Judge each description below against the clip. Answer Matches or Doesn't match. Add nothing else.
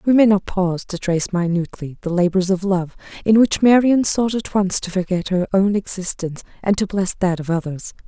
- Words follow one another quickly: Matches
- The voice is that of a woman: Matches